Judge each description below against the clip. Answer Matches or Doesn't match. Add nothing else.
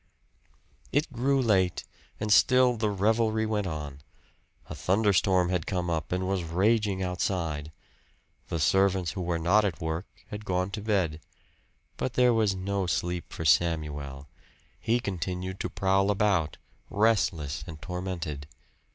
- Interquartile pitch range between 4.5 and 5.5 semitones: Doesn't match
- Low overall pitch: Matches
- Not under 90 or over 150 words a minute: Matches